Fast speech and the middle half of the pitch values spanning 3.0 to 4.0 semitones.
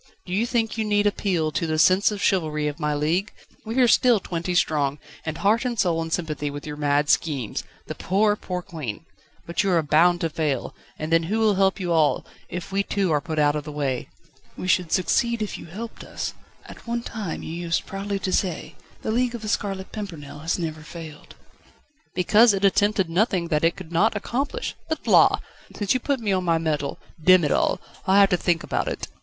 No: fast, 220 wpm; average, 4.6 semitones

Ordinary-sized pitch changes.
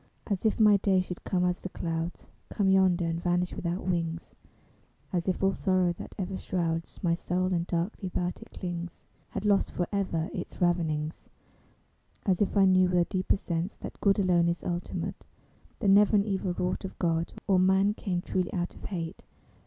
No: narrow, 1.9 semitones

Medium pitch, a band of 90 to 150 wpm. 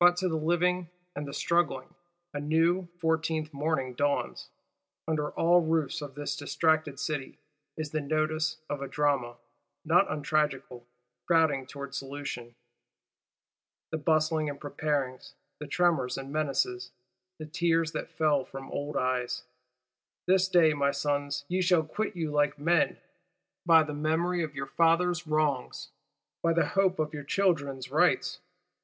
Yes: medium, 155 Hz; average, 145 wpm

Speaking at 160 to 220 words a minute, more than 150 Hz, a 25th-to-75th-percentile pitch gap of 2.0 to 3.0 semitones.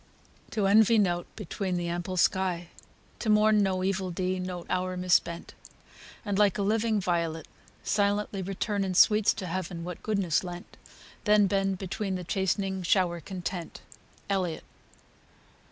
No: average, 145 wpm; high, 190 Hz; narrow, 2.4 semitones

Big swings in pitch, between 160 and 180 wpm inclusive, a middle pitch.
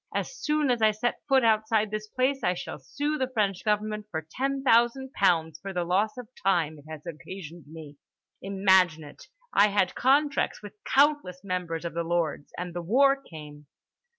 No: wide, 7.0 semitones; average, 175 wpm; high, 200 Hz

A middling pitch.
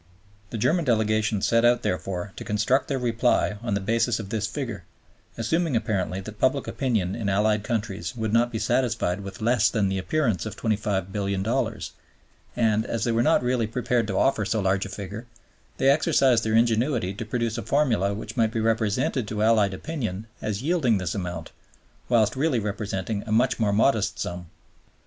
No: low, 110 Hz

